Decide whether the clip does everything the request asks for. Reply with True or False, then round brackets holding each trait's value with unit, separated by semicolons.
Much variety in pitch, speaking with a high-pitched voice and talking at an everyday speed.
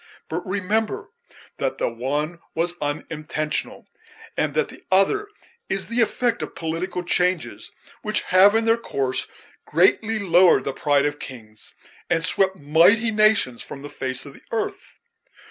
False (6.0 semitones; 175 Hz; 145 wpm)